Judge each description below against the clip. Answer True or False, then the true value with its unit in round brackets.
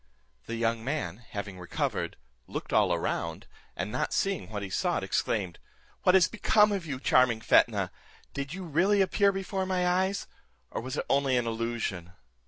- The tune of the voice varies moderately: False (8.8 semitones)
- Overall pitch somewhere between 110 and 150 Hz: True (135 Hz)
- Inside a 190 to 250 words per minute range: False (170 wpm)